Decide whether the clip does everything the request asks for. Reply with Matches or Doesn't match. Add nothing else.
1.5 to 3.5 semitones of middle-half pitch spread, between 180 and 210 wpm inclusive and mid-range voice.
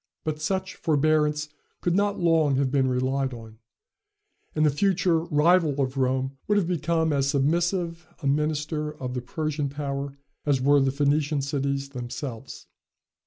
Doesn't match